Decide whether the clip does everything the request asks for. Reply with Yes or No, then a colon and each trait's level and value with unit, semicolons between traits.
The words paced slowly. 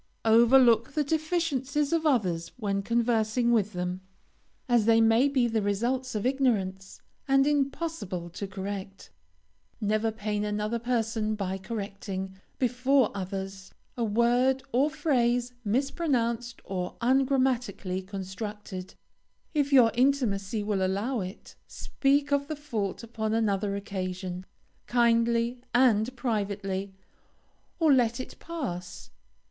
Yes: slow, 115 wpm